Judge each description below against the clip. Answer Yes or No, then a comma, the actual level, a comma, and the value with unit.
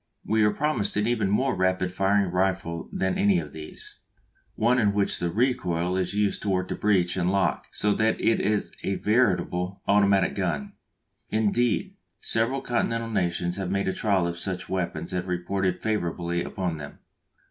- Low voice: Yes, very low, 95 Hz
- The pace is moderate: Yes, average, 170 wpm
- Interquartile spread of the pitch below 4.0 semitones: Yes, average, 2.9 semitones